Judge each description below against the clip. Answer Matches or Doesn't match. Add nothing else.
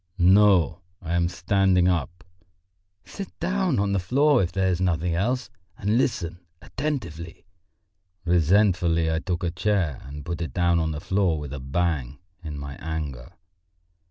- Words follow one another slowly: Doesn't match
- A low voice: Matches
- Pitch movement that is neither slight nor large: Matches